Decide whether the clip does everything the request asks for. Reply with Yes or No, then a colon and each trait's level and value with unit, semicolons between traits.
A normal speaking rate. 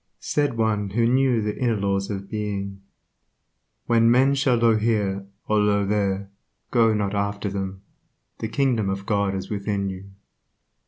Yes: average, 160 wpm